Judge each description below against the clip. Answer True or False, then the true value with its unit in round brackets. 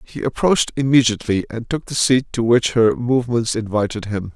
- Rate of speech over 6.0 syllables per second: False (5.5 syllables/s)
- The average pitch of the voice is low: True (115 Hz)